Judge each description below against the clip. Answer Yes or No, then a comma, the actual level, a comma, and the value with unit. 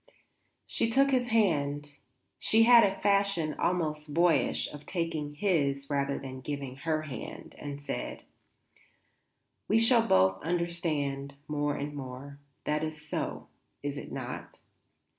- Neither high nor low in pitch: Yes, medium, 150 Hz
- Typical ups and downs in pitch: Yes, average, 4.1 semitones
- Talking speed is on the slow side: Yes, slow, 130 wpm